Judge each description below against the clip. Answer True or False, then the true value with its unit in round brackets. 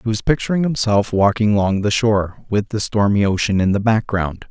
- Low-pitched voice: True (105 Hz)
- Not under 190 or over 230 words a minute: True (200 wpm)